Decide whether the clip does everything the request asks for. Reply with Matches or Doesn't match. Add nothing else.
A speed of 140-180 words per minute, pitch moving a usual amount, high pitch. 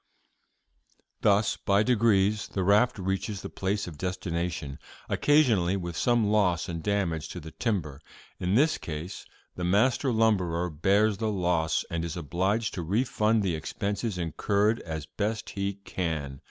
Doesn't match